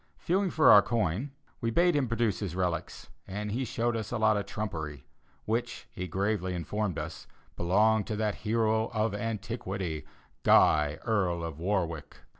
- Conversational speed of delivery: Yes, average, 160 wpm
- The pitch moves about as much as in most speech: Yes, average, 3.9 semitones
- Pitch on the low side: Yes, low, 105 Hz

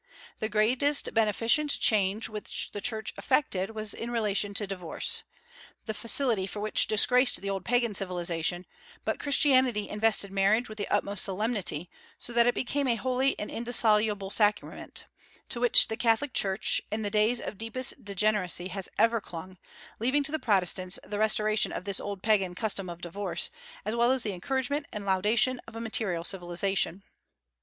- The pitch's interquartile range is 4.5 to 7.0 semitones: No, average, 3.3 semitones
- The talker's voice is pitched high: Yes, high, 215 Hz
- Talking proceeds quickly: No, average, 165 wpm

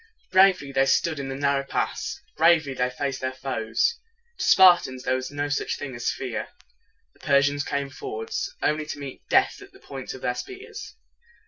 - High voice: No, medium, 140 Hz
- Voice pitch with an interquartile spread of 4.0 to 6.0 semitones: No, average, 3.5 semitones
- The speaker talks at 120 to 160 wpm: No, average, 185 wpm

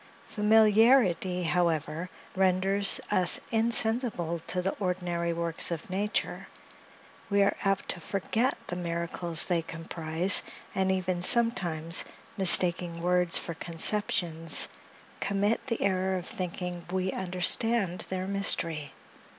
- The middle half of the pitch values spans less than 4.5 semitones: Yes, average, 2.7 semitones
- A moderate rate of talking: No, slow, 110 wpm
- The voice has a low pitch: No, medium, 180 Hz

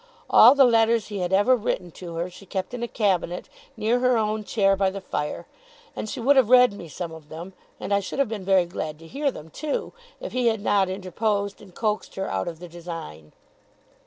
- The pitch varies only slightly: No, average, 4.6 semitones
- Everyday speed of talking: No, fast, 225 wpm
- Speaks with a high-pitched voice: Yes, high, 200 Hz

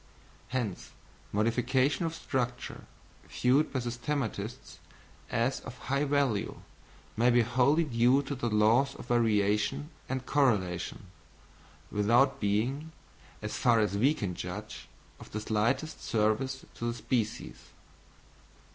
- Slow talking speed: Yes, slow, 120 wpm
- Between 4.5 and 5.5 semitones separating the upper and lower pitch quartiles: No, average, 4.0 semitones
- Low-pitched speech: Yes, low, 120 Hz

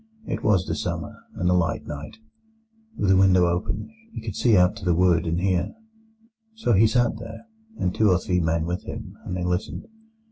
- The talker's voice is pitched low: Yes, very low, 90 Hz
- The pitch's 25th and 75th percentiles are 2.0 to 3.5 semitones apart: Yes, average, 2.9 semitones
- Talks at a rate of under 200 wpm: No, fast, 205 wpm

